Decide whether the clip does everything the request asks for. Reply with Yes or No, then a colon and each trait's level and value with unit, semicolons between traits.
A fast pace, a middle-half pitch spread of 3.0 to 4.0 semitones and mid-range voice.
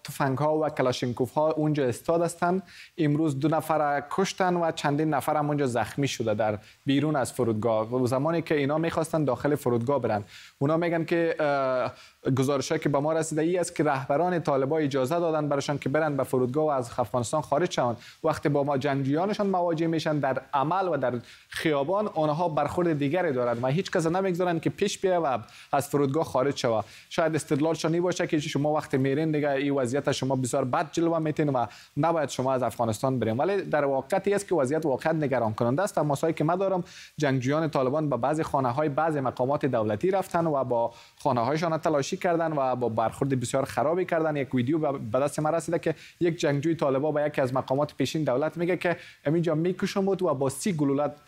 Yes: fast, 190 wpm; average, 3.5 semitones; medium, 150 Hz